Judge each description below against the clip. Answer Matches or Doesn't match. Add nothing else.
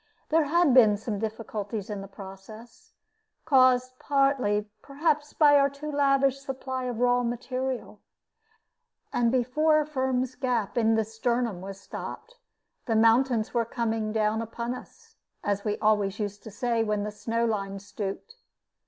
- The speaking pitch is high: Matches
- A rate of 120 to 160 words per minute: Matches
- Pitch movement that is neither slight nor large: Matches